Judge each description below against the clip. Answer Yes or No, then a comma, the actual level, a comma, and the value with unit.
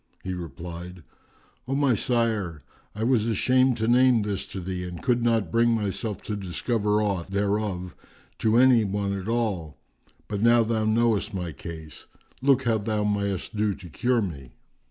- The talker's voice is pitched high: No, low, 105 Hz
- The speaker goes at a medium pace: Yes, average, 165 wpm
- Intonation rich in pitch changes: No, average, 4.0 semitones